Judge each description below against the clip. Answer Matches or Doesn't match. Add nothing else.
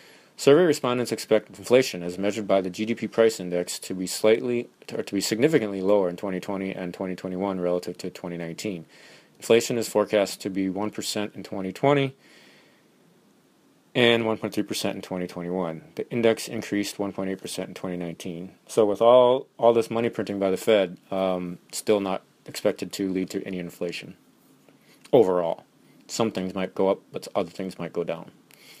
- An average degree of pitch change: Matches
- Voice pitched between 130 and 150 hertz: Doesn't match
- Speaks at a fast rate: Doesn't match